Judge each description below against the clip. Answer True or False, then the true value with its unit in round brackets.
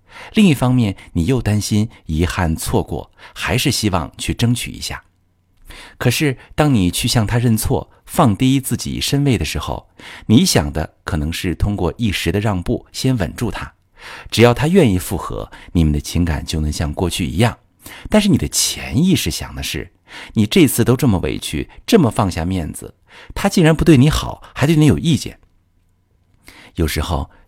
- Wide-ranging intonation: True (6.7 semitones)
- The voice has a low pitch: True (100 Hz)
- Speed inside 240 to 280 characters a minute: True (250 characters per minute)